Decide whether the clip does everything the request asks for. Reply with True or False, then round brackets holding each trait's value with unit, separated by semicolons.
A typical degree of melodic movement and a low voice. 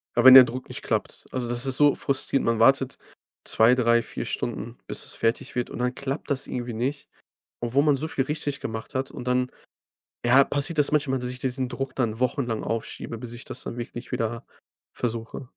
False (2.3 semitones; 125 Hz)